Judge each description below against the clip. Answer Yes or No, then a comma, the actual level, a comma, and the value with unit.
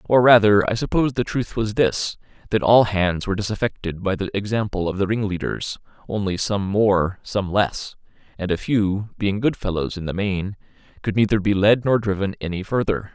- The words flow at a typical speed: Yes, average, 185 wpm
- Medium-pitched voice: No, low, 100 Hz